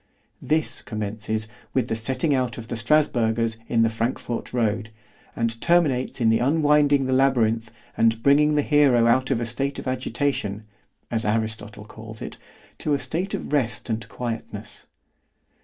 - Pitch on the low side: Yes, low, 120 Hz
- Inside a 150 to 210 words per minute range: Yes, average, 155 wpm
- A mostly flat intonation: No, average, 3.8 semitones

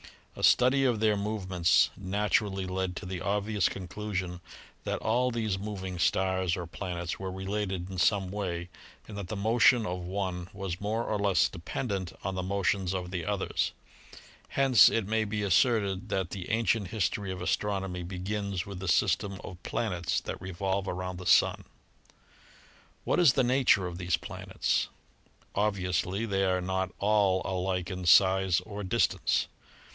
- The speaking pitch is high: No, very low, 95 Hz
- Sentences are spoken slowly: No, average, 160 wpm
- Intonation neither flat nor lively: No, narrow, 2.2 semitones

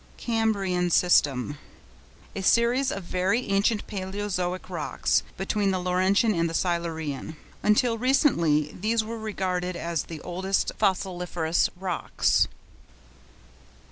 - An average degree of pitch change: Yes, average, 3.6 semitones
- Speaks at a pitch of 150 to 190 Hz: Yes, medium, 185 Hz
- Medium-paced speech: No, slow, 105 wpm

